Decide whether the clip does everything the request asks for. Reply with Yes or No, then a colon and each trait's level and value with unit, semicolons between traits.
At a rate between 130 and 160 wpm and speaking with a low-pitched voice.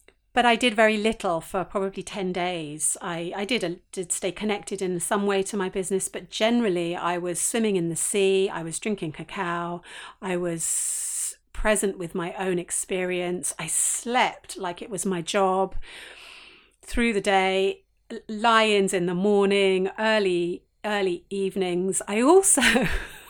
No: average, 155 wpm; high, 190 Hz